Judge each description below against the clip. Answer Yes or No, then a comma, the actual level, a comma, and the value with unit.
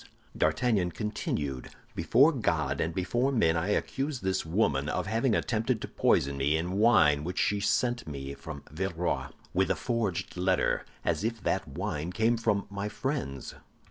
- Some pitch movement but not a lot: No, wide, 6.2 semitones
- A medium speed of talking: Yes, average, 160 wpm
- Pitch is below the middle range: Yes, very low, 95 Hz